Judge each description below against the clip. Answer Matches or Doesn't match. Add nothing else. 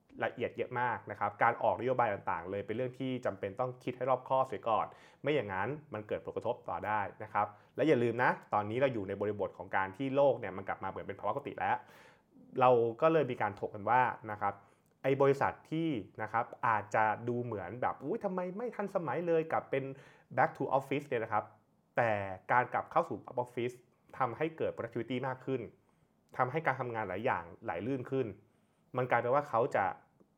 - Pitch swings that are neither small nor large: Matches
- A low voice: Matches